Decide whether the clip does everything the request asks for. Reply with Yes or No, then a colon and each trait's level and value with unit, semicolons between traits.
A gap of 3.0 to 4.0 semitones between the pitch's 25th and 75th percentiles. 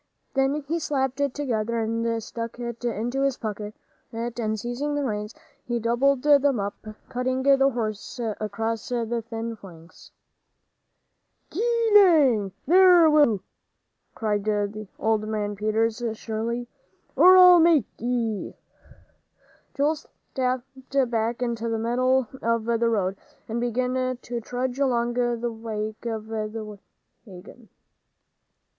Yes: average, 3.3 semitones